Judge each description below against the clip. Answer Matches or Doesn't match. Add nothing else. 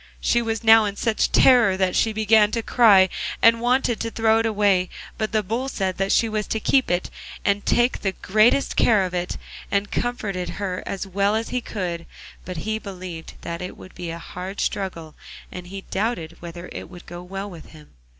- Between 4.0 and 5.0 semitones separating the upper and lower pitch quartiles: Doesn't match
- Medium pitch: Doesn't match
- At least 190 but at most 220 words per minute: Matches